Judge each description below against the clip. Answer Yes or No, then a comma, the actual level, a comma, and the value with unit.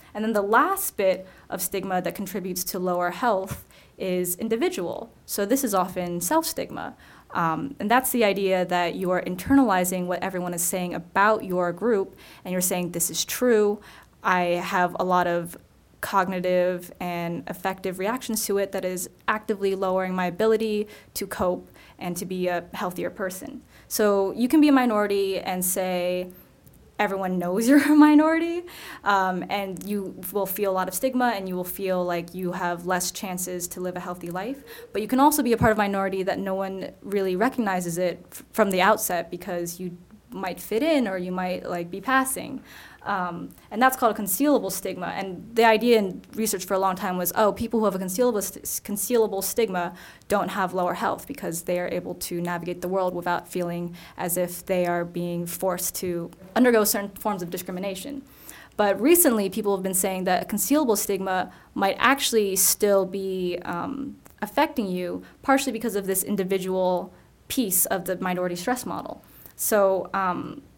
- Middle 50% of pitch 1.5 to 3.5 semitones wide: Yes, average, 3.2 semitones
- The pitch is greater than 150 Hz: Yes, high, 190 Hz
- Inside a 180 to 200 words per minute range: Yes, average, 185 wpm